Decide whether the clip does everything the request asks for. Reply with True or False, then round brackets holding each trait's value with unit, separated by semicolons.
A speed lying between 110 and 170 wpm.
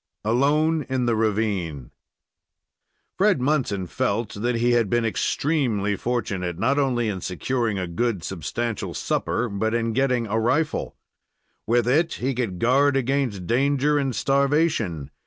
True (140 wpm)